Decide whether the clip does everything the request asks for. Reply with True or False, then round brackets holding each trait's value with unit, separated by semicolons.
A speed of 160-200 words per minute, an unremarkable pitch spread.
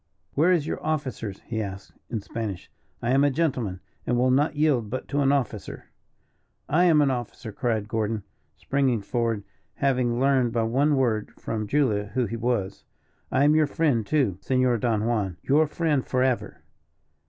True (170 wpm; 4.2 semitones)